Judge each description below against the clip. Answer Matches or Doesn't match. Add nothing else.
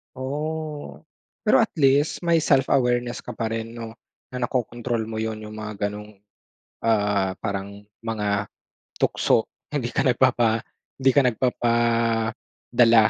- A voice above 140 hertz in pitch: Doesn't match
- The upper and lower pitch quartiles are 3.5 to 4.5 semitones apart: Doesn't match